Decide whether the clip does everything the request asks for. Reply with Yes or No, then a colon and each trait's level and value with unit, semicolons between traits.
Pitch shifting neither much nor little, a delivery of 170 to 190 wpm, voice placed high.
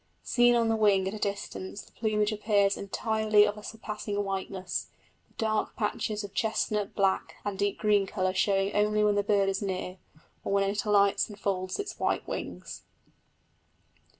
No: narrow, 1.3 semitones; average, 175 wpm; high, 205 Hz